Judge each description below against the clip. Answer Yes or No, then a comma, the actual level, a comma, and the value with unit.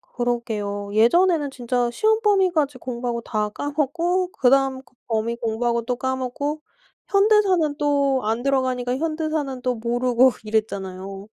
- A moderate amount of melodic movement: Yes, average, 4.1 semitones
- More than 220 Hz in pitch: Yes, very high, 255 Hz